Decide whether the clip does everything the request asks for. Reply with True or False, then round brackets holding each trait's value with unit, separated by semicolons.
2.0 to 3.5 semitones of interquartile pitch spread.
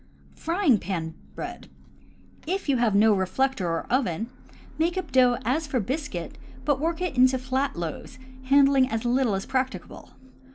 False (4.3 semitones)